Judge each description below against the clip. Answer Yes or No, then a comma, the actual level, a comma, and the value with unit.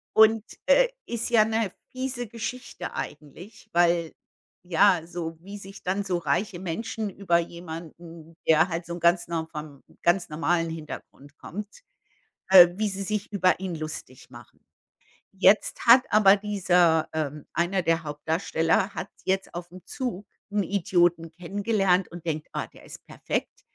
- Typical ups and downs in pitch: Yes, average, 3.6 semitones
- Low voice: No, medium, 180 Hz